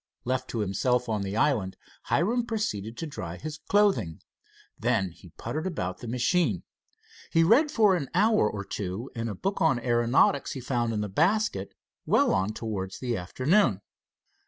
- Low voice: Yes, low, 120 Hz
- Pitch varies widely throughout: Yes, wide, 8.3 semitones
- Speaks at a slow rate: No, average, 165 wpm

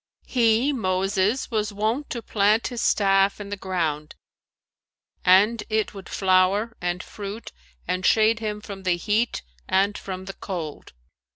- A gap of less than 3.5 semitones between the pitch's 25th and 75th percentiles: Yes, average, 2.7 semitones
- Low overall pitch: No, high, 200 Hz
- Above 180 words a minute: No, average, 150 wpm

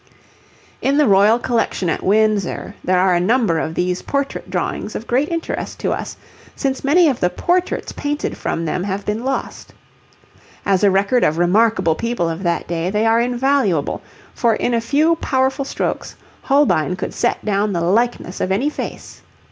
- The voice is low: No, high, 215 Hz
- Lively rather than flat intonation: Yes, wide, 6.5 semitones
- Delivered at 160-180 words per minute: Yes, average, 175 wpm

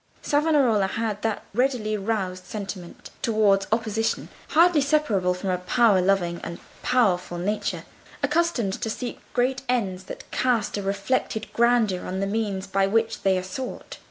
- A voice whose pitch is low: No, high, 215 Hz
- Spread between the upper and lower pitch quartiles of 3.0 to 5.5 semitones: Yes, average, 4.1 semitones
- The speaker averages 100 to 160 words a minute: Yes, average, 150 wpm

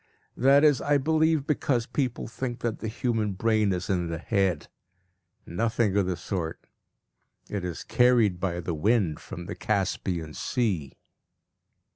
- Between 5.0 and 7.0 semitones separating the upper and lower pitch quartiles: Yes, wide, 5.5 semitones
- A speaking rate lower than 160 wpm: Yes, average, 145 wpm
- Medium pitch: No, low, 105 Hz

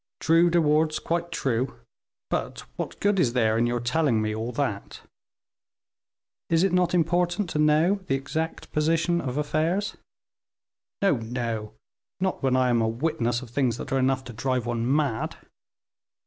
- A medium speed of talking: Yes, average, 160 wpm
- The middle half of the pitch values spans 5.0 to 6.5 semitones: Yes, wide, 5.6 semitones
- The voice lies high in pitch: No, low, 135 Hz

